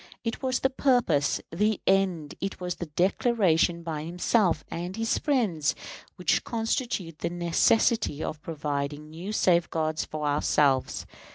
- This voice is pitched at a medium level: Yes, medium, 175 Hz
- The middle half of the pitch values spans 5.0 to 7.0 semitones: Yes, wide, 5.6 semitones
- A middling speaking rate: No, slow, 130 wpm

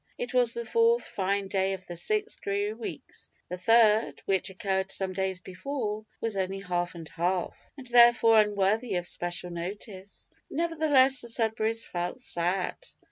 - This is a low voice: No, high, 200 Hz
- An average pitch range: Yes, average, 4.1 semitones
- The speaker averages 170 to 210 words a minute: No, average, 155 wpm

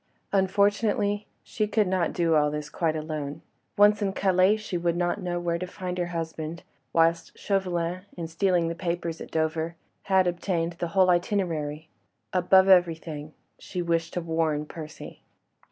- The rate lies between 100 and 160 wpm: Yes, average, 155 wpm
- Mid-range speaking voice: Yes, medium, 175 Hz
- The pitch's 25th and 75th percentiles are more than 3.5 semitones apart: No, narrow, 2.5 semitones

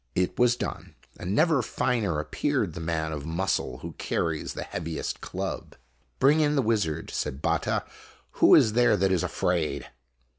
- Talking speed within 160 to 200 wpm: Yes, average, 170 wpm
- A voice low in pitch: Yes, very low, 90 Hz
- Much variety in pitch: Yes, wide, 7.0 semitones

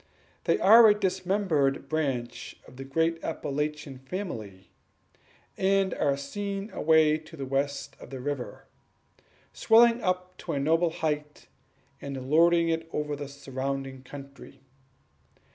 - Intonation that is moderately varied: Yes, average, 4.7 semitones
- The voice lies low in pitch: No, medium, 150 Hz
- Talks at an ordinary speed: No, slow, 125 wpm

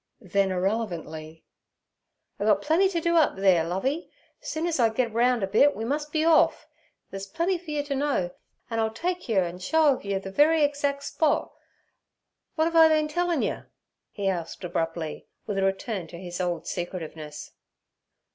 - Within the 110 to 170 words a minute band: No, average, 180 wpm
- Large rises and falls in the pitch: Yes, wide, 8.6 semitones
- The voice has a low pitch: No, high, 225 Hz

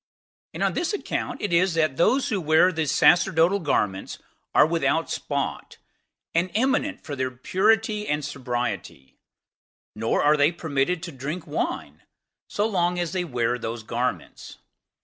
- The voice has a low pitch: No, medium, 160 Hz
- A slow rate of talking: No, average, 150 wpm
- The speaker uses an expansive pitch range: Yes, wide, 5.9 semitones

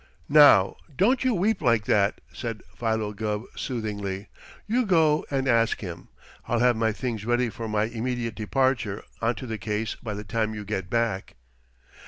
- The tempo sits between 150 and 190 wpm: Yes, average, 165 wpm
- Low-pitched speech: Yes, low, 115 Hz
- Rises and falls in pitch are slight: No, average, 3.0 semitones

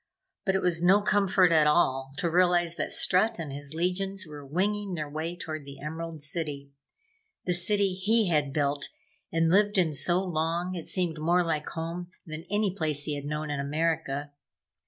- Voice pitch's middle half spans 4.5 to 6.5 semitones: No, average, 3.4 semitones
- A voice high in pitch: No, medium, 165 Hz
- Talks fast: No, average, 180 wpm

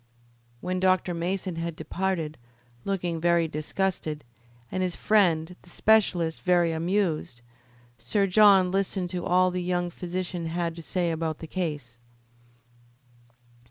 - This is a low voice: No, medium, 175 Hz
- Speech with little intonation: Yes, narrow, 2.2 semitones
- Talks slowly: Yes, slow, 125 wpm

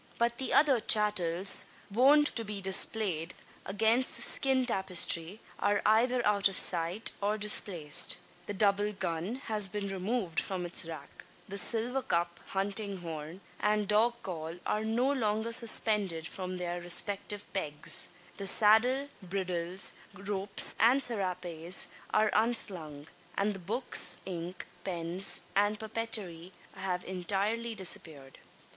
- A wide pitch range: No, average, 3.7 semitones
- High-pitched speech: Yes, high, 200 Hz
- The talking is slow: Yes, slow, 130 wpm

